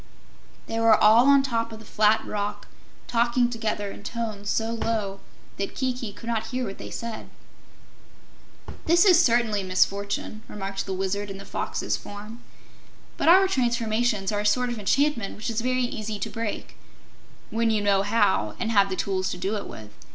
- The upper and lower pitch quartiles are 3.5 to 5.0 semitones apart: No, average, 2.8 semitones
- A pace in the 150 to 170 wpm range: No, average, 180 wpm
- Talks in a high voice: Yes, high, 220 Hz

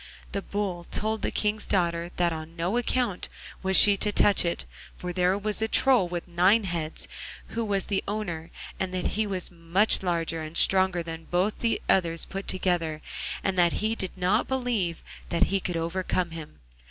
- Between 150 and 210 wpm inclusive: Yes, average, 185 wpm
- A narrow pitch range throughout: No, average, 3.3 semitones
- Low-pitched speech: No, medium, 185 Hz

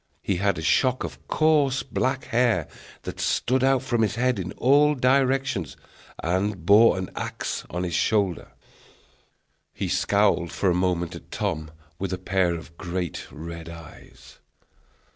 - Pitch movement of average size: No, wide, 6.5 semitones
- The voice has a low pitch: Yes, low, 100 Hz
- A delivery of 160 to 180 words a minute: No, average, 150 wpm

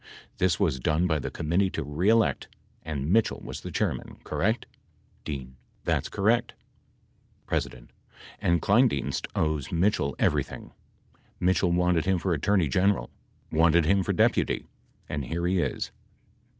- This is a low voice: Yes, very low, 85 Hz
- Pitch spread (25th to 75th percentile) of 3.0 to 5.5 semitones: Yes, average, 4.1 semitones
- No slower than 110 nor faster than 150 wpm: Yes, average, 140 wpm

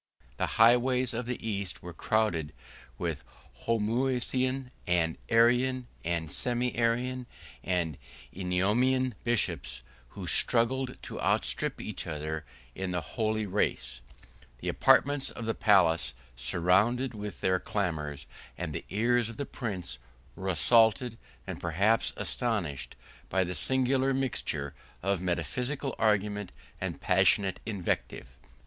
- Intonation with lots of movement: Yes, wide, 5.7 semitones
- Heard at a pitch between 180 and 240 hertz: No, low, 105 Hz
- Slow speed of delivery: Yes, slow, 120 wpm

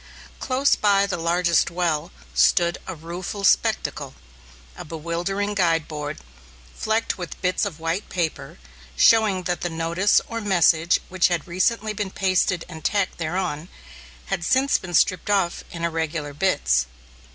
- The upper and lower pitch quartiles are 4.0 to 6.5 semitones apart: No, average, 3.2 semitones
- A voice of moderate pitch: Yes, medium, 175 Hz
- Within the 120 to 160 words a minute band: Yes, average, 140 wpm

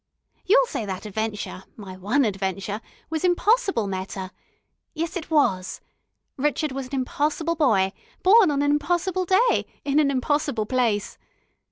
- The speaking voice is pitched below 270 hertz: No, very high, 275 Hz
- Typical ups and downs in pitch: No, wide, 8.2 semitones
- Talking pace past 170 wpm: No, average, 140 wpm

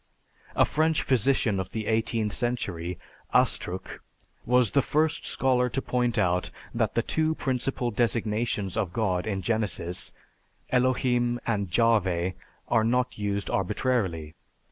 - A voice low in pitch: Yes, low, 115 Hz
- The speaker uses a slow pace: Yes, slow, 125 wpm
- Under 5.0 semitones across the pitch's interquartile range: Yes, average, 4.6 semitones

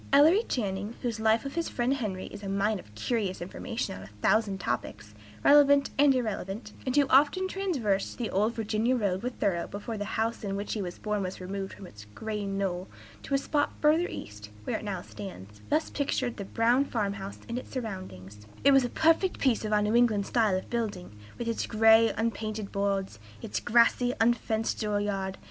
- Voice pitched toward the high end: Yes, high, 215 Hz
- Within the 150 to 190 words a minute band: No, average, 200 wpm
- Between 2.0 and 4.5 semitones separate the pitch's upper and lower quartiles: Yes, average, 4.0 semitones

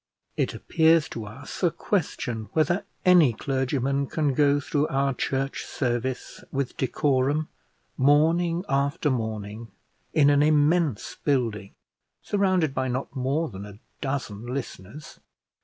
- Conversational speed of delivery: No, slow, 125 wpm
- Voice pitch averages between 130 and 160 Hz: Yes, medium, 140 Hz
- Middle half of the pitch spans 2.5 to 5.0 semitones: Yes, average, 3.7 semitones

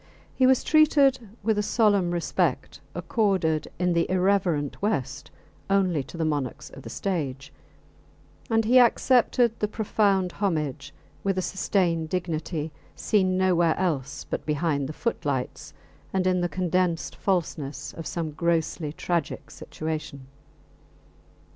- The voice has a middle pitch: Yes, medium, 175 Hz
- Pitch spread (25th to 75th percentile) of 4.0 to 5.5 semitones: Yes, average, 4.3 semitones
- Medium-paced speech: No, slow, 130 wpm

